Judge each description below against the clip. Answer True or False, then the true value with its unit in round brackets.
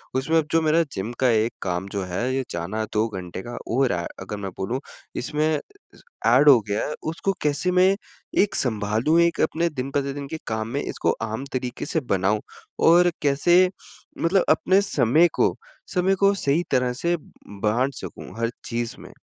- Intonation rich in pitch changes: True (7.0 semitones)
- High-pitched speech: False (130 Hz)